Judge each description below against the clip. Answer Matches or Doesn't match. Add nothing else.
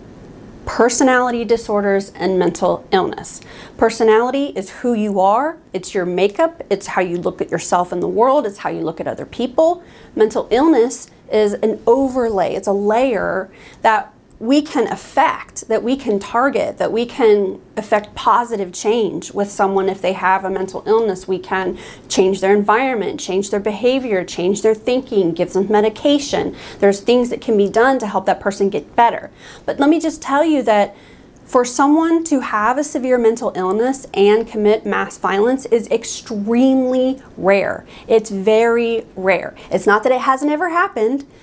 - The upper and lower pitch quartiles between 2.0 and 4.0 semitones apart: Doesn't match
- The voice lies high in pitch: Matches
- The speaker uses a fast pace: Doesn't match